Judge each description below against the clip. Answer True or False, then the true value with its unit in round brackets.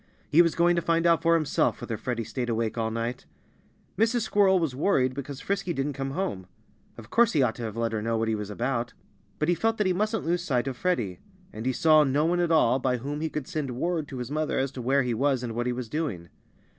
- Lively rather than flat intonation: True (5.9 semitones)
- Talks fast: True (255 wpm)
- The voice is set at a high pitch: False (135 Hz)